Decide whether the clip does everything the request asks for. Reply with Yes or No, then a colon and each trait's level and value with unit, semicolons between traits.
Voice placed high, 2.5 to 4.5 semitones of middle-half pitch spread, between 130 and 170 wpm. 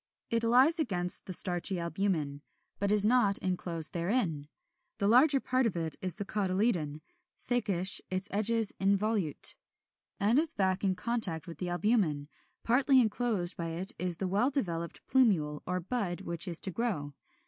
No: high, 195 Hz; average, 5.0 semitones; average, 160 wpm